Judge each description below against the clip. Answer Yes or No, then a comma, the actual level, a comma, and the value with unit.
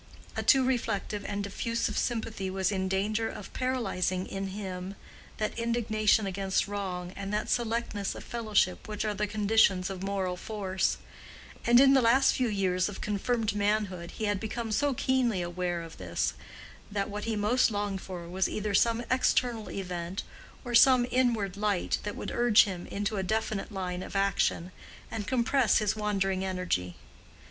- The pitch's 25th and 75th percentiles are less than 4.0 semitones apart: Yes, average, 3.1 semitones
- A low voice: No, high, 205 Hz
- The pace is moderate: Yes, average, 165 wpm